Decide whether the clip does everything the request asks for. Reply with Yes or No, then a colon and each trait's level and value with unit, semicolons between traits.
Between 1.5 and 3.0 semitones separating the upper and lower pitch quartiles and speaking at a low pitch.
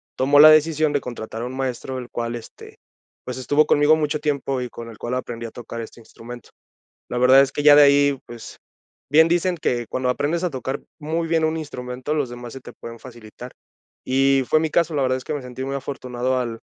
No: average, 3.4 semitones; low, 130 Hz